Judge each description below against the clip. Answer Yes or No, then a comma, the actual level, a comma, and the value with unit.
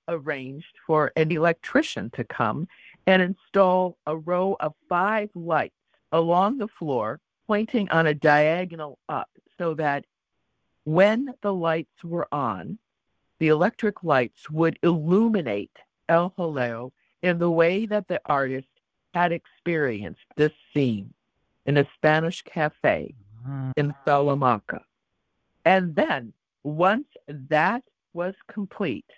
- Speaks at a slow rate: Yes, slow, 115 wpm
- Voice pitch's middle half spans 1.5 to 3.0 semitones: No, average, 3.8 semitones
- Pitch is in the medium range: Yes, medium, 165 Hz